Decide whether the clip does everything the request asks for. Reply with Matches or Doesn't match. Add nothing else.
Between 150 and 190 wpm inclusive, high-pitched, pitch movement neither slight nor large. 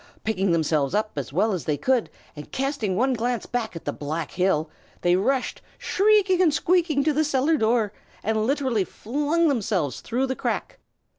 Doesn't match